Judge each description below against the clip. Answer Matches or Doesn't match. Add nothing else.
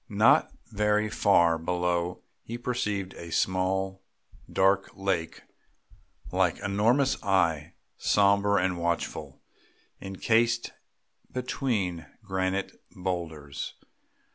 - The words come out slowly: Matches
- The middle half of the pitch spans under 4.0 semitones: Matches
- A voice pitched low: Matches